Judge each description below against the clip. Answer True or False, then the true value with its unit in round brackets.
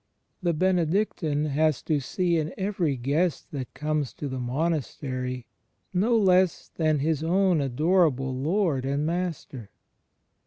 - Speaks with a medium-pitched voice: True (155 Hz)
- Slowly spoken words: True (130 wpm)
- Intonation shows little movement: False (4.6 semitones)